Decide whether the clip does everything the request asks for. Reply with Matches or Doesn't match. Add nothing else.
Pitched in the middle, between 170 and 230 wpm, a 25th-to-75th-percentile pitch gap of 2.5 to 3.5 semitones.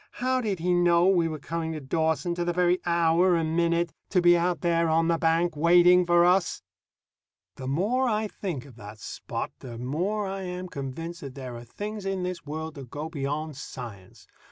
Matches